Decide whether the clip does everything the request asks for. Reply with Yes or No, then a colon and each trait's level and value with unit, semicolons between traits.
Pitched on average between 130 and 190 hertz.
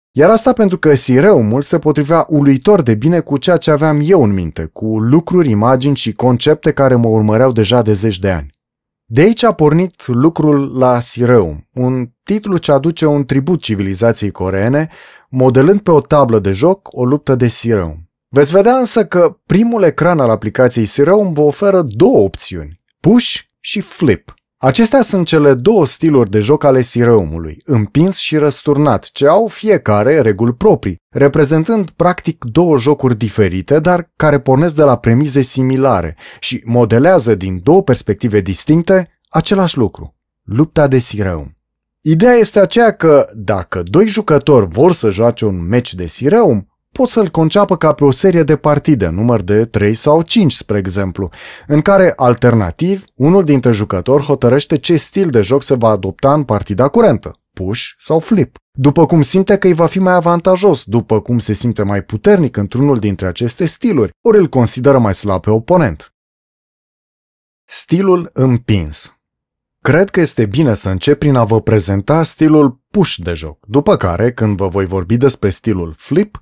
Yes: low, 135 Hz